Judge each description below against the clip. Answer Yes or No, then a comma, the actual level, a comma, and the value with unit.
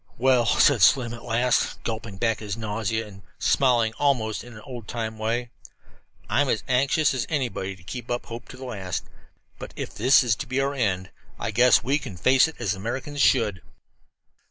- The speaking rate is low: No, average, 190 wpm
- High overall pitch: No, low, 120 Hz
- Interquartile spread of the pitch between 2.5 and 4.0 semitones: Yes, average, 2.9 semitones